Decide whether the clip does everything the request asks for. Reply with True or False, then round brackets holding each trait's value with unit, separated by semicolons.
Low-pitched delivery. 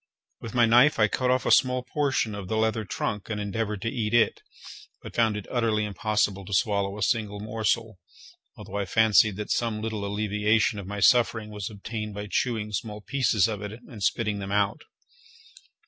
True (105 Hz)